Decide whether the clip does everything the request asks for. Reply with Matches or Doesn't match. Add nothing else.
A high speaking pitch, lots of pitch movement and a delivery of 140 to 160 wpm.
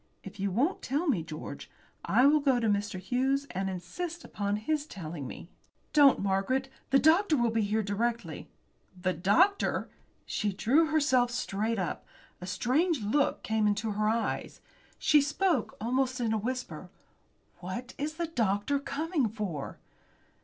Matches